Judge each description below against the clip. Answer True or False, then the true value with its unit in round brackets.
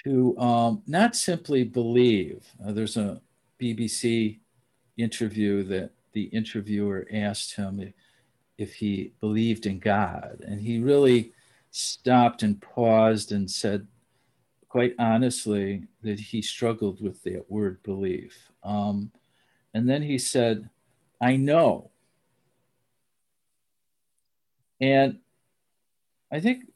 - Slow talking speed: True (110 wpm)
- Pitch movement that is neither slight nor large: True (3.2 semitones)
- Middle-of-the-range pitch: False (115 Hz)